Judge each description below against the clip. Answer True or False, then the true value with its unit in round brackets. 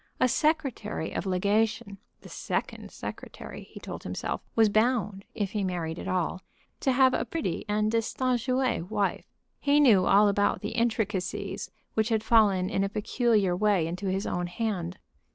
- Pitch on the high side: True (210 Hz)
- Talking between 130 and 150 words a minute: False (160 wpm)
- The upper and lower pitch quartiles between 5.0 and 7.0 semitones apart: False (3.5 semitones)